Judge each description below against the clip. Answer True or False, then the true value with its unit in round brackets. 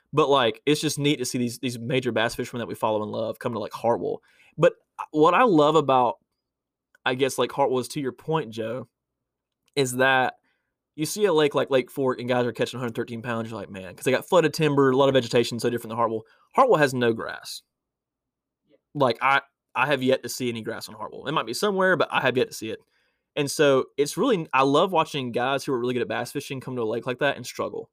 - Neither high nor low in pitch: False (130 Hz)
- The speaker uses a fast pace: True (245 wpm)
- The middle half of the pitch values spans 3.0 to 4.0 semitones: True (3.6 semitones)